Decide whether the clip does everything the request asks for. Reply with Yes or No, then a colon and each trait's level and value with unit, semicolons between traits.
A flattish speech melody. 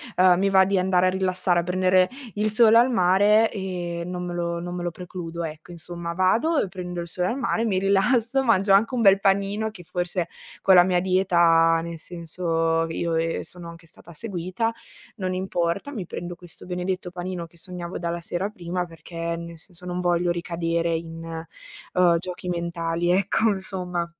Yes: narrow, 2.0 semitones